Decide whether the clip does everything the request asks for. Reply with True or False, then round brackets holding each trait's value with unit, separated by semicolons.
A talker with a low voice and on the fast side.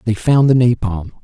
False (115 Hz; 195 wpm)